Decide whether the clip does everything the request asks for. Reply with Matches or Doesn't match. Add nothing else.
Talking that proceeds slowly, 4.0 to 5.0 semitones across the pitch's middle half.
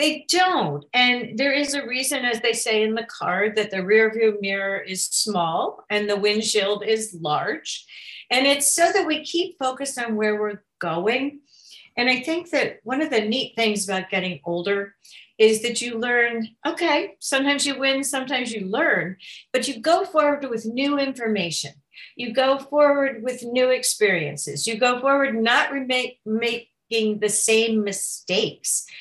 Doesn't match